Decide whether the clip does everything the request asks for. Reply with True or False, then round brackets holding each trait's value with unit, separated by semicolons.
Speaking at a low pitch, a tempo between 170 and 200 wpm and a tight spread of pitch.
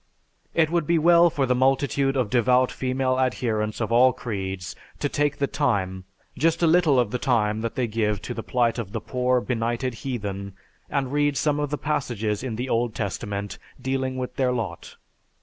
False (125 Hz; 185 wpm; 3.8 semitones)